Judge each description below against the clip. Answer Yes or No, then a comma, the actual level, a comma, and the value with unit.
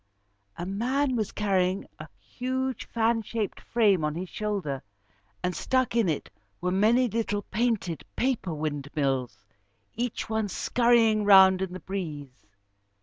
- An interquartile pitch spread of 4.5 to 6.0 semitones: Yes, average, 4.8 semitones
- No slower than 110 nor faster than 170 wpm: Yes, slow, 135 wpm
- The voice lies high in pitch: Yes, high, 200 Hz